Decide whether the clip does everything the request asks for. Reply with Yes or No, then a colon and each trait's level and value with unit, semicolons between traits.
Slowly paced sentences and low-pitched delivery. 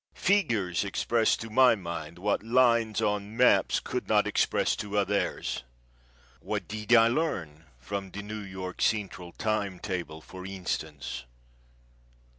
Yes: slow, 130 wpm; low, 100 Hz